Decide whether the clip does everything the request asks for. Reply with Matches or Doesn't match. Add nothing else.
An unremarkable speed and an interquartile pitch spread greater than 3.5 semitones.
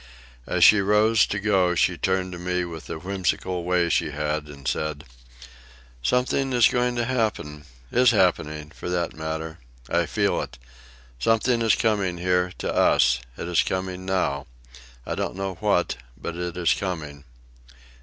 Matches